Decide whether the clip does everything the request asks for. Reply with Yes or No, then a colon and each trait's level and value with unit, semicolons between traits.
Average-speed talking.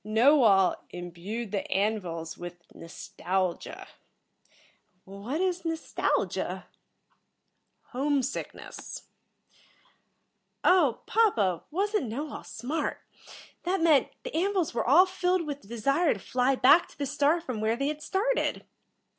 No: slow, 120 wpm